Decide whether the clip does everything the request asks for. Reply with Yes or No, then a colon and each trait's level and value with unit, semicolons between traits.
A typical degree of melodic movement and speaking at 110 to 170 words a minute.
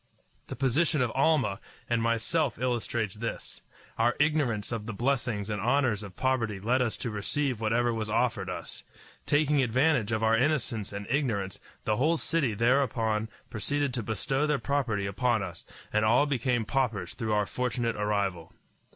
Yes: average, 4.0 semitones; average, 160 wpm